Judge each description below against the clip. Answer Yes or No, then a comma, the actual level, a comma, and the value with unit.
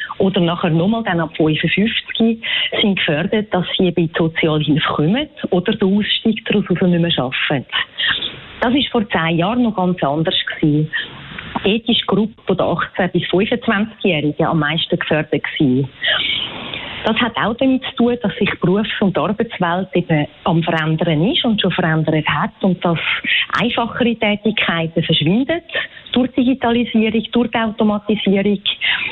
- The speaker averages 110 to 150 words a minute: Yes, average, 145 wpm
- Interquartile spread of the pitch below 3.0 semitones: No, average, 5.3 semitones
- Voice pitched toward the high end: Yes, high, 195 Hz